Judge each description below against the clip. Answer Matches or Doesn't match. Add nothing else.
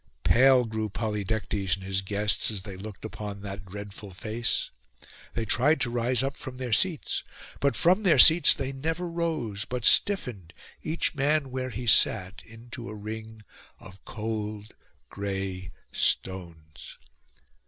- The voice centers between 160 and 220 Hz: Doesn't match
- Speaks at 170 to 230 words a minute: Doesn't match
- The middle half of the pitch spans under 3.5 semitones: Doesn't match